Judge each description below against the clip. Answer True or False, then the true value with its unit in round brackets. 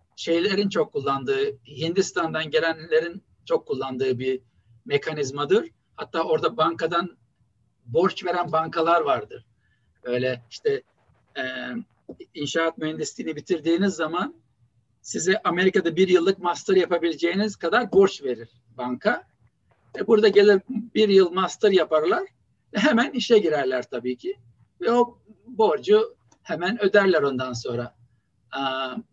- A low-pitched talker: False (170 Hz)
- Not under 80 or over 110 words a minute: True (105 wpm)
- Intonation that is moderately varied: False (9.0 semitones)